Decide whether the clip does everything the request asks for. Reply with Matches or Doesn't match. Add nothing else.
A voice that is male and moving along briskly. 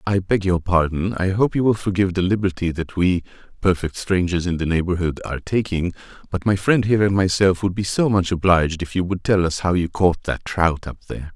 Matches